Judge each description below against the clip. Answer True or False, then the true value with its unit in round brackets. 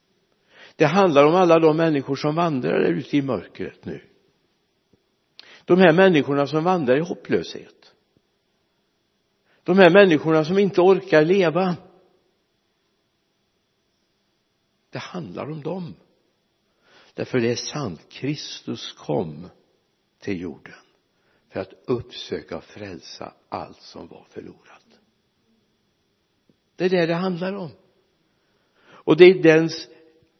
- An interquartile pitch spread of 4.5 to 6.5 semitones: False (3.3 semitones)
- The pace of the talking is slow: True (110 wpm)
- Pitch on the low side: False (165 Hz)